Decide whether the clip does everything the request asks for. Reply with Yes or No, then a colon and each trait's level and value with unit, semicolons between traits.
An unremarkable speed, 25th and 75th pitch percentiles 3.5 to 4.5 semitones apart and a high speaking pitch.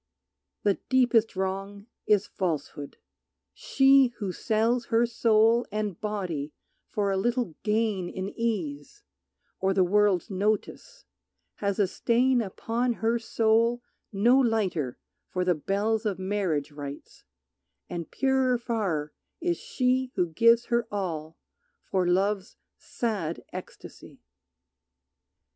No: slow, 115 wpm; average, 3.9 semitones; high, 210 Hz